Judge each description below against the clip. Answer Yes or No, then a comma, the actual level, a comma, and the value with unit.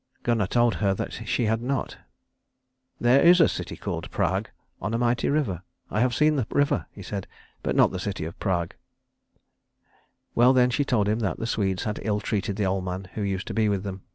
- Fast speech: Yes, fast, 210 wpm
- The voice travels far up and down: No, average, 3.9 semitones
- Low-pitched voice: Yes, low, 105 Hz